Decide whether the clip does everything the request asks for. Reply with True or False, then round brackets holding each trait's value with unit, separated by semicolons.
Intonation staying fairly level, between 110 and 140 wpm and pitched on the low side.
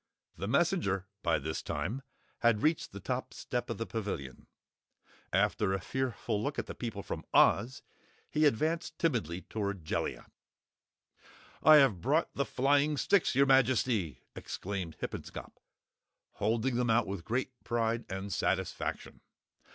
False (5.5 semitones; 135 wpm; 115 Hz)